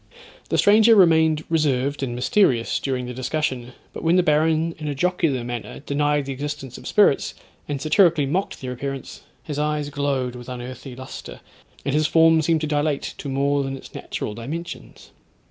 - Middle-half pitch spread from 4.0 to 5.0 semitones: No, average, 3.4 semitones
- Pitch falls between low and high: Yes, medium, 145 Hz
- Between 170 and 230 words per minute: Yes, average, 175 wpm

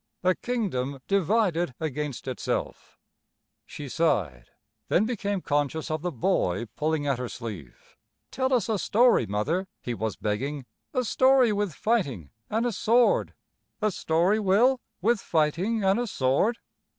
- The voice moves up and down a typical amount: No, wide, 8.3 semitones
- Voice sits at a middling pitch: Yes, medium, 175 Hz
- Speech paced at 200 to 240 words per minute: No, average, 140 wpm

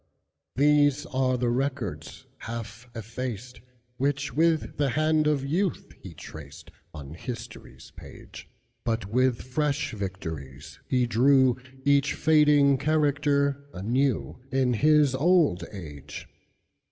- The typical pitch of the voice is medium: No, low, 130 Hz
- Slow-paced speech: Yes, slow, 90 wpm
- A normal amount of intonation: Yes, average, 4.1 semitones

